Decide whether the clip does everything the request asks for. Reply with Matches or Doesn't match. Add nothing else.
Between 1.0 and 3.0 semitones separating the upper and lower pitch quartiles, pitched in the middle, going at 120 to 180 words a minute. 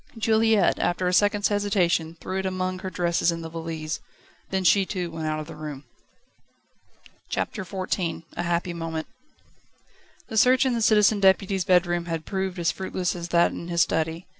Matches